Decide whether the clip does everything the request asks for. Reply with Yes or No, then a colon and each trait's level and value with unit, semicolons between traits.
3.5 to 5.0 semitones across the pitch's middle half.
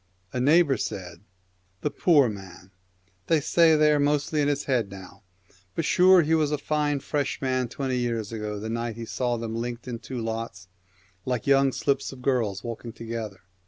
Yes: average, 4.4 semitones